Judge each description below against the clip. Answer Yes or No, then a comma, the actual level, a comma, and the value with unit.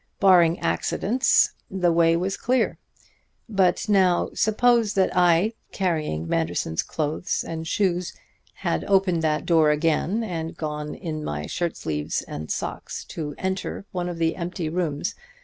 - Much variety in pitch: No, average, 3.5 semitones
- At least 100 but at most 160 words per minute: Yes, average, 140 wpm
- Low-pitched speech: No, medium, 170 Hz